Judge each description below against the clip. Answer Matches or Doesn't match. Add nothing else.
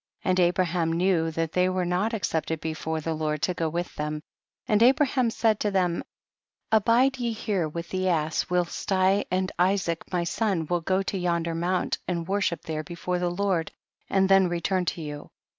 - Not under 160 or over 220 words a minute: Matches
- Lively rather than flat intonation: Doesn't match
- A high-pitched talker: Doesn't match